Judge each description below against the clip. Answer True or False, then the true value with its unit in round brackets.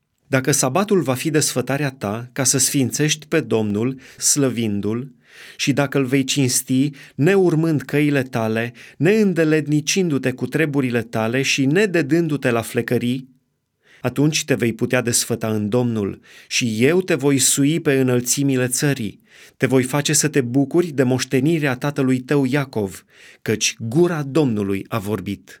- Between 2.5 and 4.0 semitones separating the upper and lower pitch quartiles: True (3.2 semitones)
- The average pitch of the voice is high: False (135 Hz)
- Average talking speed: True (140 wpm)